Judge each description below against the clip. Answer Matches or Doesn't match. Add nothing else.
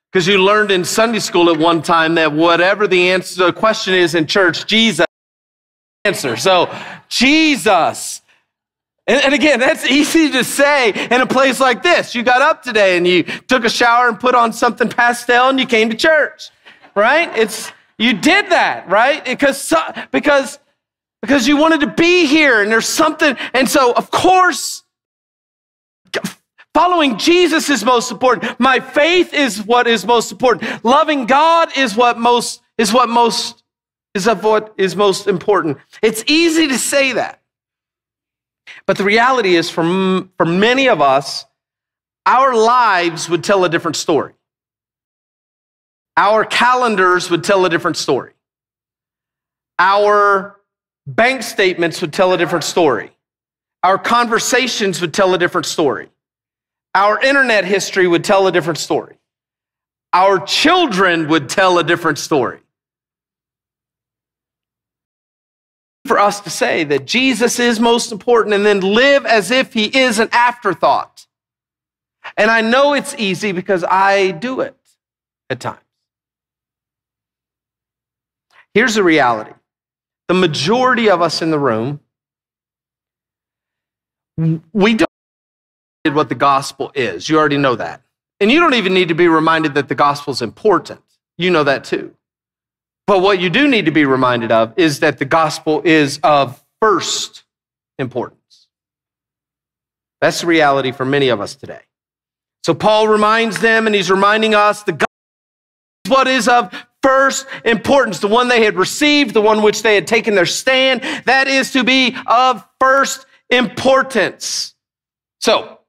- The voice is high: Matches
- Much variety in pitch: Matches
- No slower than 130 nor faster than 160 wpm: Matches